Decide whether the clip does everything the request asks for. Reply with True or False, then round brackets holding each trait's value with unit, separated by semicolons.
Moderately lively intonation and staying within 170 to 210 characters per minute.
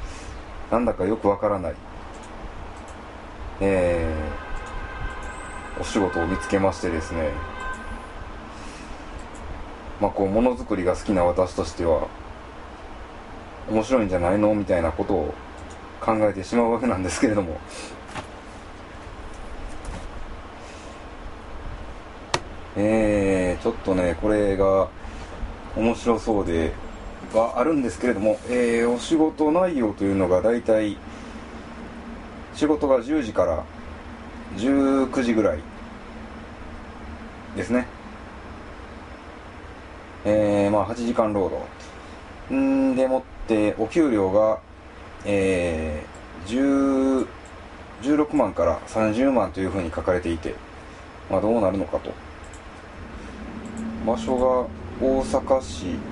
False (5.9 semitones; 190 characters per minute)